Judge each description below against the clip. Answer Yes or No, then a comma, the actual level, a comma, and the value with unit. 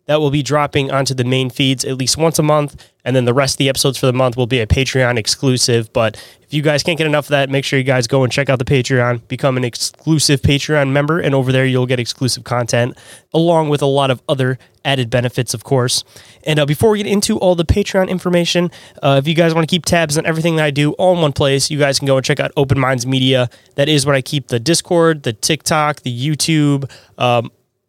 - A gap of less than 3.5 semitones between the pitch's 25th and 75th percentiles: Yes, average, 2.9 semitones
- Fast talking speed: Yes, fast, 255 wpm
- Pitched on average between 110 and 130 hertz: No, medium, 140 Hz